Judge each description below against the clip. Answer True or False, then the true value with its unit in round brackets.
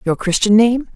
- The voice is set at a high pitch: True (220 Hz)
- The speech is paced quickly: False (190 wpm)